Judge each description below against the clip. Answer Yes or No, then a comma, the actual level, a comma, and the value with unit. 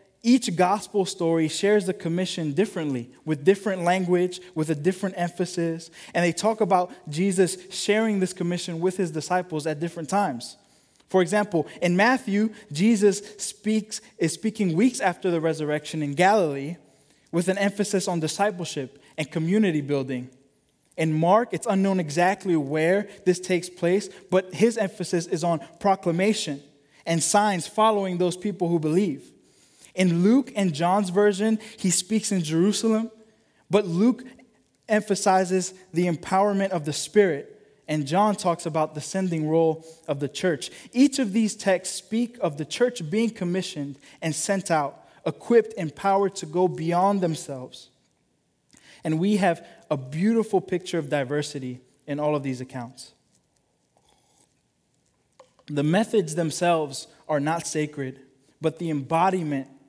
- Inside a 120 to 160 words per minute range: Yes, average, 140 wpm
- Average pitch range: Yes, average, 4.1 semitones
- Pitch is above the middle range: No, medium, 180 Hz